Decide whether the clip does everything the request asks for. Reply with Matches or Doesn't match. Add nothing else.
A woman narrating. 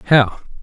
Doesn't match